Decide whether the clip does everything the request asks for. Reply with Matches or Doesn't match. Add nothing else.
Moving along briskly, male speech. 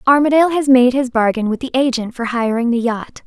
Doesn't match